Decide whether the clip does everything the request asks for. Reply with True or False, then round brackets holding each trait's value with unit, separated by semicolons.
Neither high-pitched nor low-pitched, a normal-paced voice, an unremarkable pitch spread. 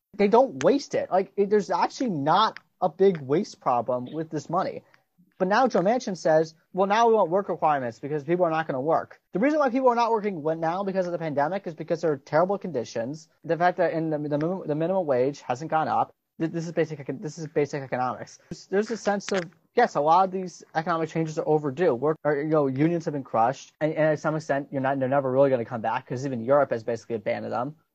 False (160 Hz; 235 wpm; 4.3 semitones)